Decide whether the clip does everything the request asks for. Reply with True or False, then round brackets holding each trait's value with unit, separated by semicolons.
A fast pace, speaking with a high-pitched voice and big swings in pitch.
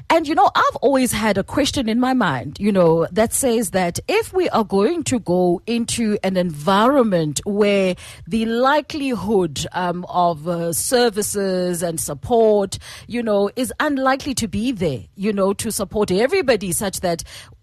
False (165 wpm; 205 Hz; 5.8 semitones)